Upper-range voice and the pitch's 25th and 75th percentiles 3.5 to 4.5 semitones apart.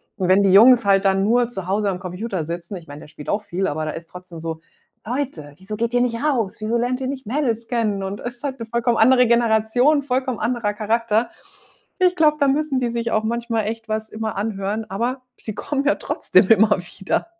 Yes: high, 225 Hz; average, 3.9 semitones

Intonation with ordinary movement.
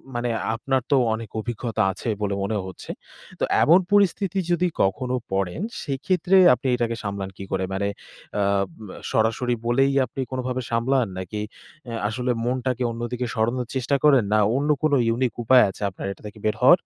Yes: average, 3.5 semitones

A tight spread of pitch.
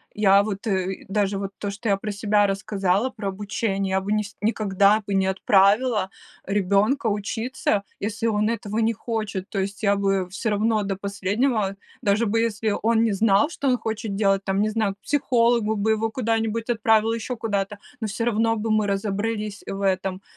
Yes: narrow, 2.2 semitones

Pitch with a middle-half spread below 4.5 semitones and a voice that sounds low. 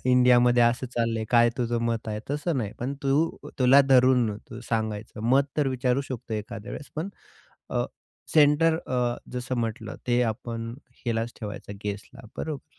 Yes: narrow, 2.5 semitones; low, 120 Hz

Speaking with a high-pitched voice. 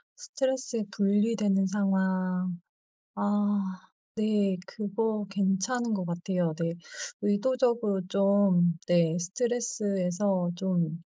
Yes: high, 200 Hz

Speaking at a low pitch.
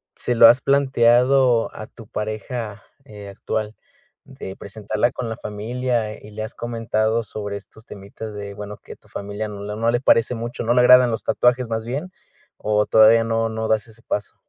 Yes: low, 110 Hz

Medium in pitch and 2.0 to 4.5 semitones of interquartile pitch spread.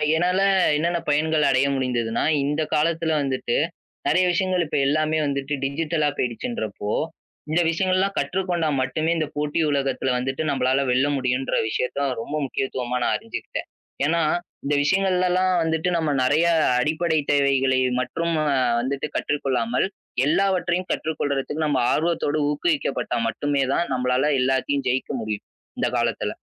Yes: medium, 145 Hz; average, 3.9 semitones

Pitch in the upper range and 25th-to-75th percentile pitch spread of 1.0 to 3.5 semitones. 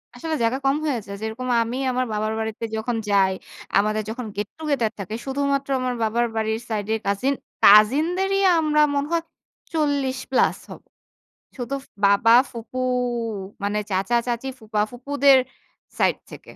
No: high, 240 Hz; average, 4.3 semitones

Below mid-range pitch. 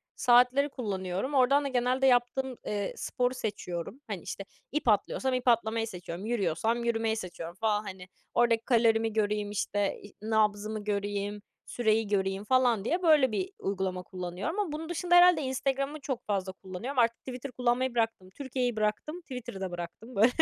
No: high, 225 Hz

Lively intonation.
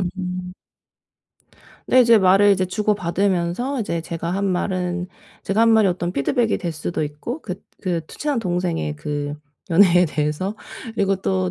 No: average, 3.1 semitones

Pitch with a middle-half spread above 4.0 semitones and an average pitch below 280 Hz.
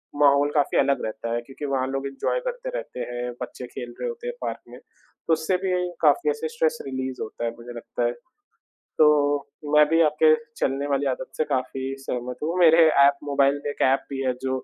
No: average, 3.4 semitones; medium, 140 Hz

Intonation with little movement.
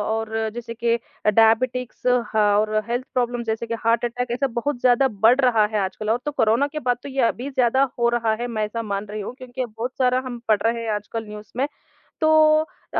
Yes: narrow, 2.2 semitones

